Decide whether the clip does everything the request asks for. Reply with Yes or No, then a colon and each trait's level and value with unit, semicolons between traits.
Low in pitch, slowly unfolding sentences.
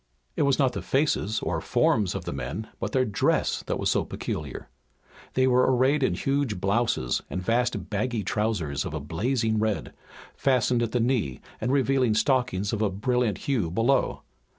No: low, 115 Hz; average, 175 wpm